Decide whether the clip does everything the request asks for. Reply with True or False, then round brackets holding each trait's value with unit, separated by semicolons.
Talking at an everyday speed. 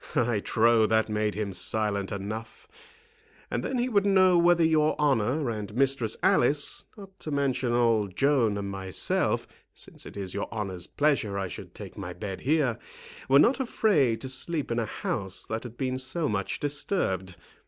True (175 wpm)